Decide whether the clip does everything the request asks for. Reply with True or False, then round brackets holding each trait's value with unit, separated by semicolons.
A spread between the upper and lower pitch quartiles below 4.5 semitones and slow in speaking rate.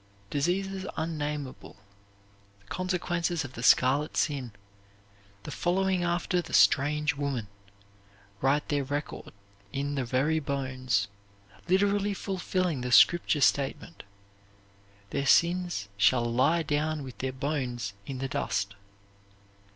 False (4.8 semitones; 110 wpm)